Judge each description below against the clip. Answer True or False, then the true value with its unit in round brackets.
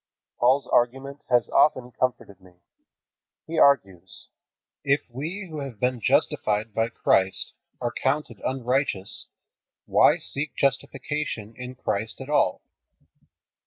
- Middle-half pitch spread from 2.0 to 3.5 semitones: False (4.1 semitones)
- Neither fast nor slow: False (115 wpm)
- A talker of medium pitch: False (125 Hz)